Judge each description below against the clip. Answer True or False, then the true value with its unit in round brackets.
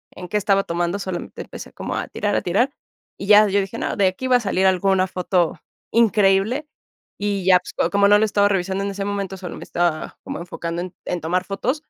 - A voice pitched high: True (195 Hz)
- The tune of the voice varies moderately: False (2.1 semitones)